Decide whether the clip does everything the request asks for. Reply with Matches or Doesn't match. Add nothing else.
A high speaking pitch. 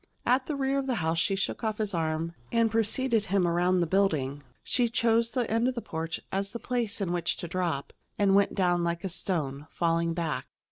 Matches